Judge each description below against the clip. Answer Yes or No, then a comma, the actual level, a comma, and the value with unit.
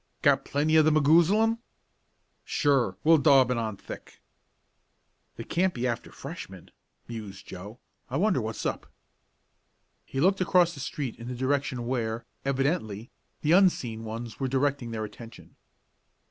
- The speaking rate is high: No, average, 145 wpm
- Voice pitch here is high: No, low, 135 Hz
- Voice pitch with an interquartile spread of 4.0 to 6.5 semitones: Yes, average, 5.3 semitones